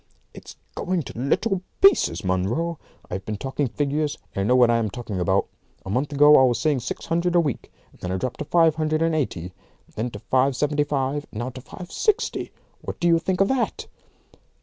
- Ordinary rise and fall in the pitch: No, wide, 5.8 semitones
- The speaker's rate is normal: No, fast, 215 wpm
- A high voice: No, medium, 140 Hz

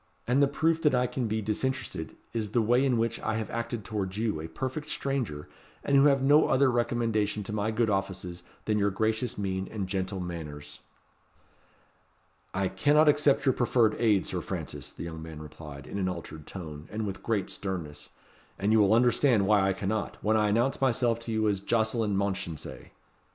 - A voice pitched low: Yes, low, 110 Hz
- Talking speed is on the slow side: No, average, 190 wpm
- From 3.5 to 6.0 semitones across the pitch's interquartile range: Yes, average, 4.0 semitones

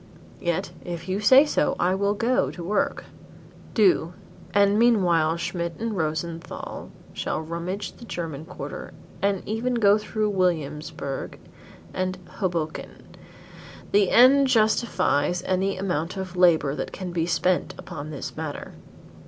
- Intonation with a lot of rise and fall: No, average, 3.8 semitones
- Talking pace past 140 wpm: No, slow, 135 wpm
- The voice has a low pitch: No, medium, 185 Hz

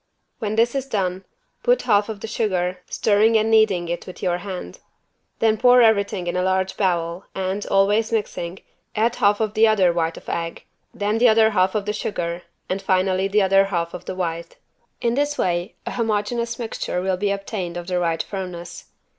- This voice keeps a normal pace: Yes, average, 190 wpm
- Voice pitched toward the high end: Yes, high, 195 Hz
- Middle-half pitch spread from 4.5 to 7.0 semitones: No, average, 3.3 semitones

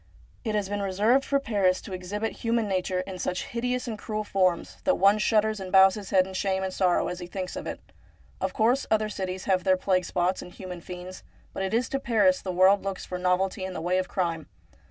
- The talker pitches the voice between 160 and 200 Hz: Yes, high, 190 Hz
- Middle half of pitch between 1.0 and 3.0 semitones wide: Yes, narrow, 2.6 semitones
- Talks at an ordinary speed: No, fast, 235 wpm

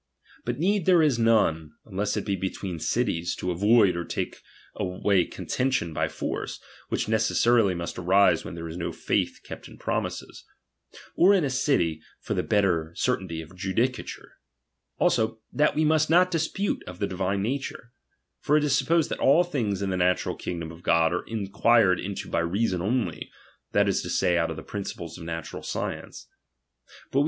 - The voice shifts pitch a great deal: Yes, wide, 6.6 semitones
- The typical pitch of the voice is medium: No, low, 100 Hz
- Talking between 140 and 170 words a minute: No, average, 180 wpm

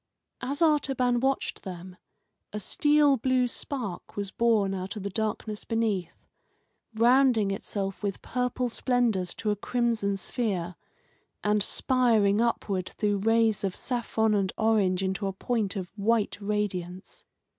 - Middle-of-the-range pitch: No, high, 215 Hz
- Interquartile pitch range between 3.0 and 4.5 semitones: Yes, average, 3.7 semitones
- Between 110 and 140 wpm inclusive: Yes, slow, 135 wpm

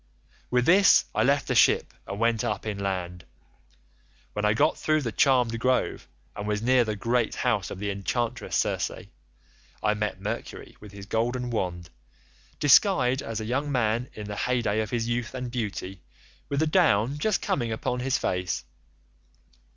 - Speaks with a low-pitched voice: Yes, low, 115 Hz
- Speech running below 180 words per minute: Yes, average, 170 wpm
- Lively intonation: No, average, 3.5 semitones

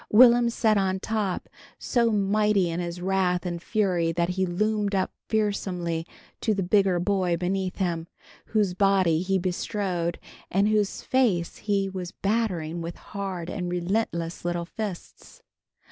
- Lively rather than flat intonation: No, average, 3.0 semitones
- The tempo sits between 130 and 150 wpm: Yes, average, 145 wpm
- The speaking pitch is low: No, high, 190 Hz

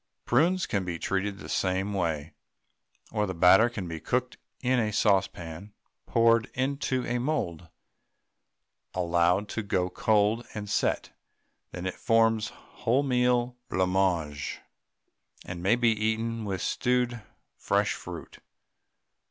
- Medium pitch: No, low, 105 Hz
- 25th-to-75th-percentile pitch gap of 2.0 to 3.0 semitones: No, average, 4.6 semitones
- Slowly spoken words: Yes, slow, 120 wpm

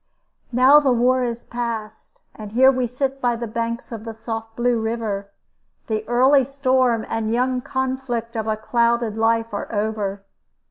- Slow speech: No, average, 165 wpm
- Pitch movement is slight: Yes, narrow, 2.3 semitones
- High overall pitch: Yes, high, 235 Hz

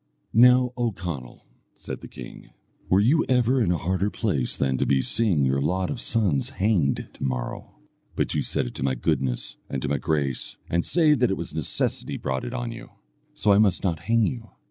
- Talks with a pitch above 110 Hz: No, very low, 95 Hz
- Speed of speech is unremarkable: No, fast, 210 wpm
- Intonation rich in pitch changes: Yes, wide, 8.9 semitones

